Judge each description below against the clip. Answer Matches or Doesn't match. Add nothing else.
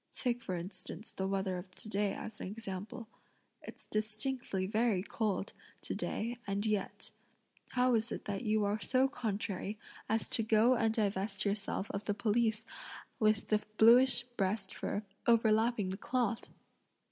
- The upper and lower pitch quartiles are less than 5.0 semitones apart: Matches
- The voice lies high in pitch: Matches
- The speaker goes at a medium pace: Matches